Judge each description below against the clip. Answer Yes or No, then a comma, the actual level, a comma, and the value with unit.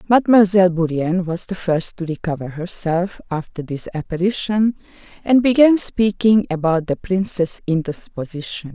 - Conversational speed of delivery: No, slow, 125 wpm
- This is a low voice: No, medium, 180 Hz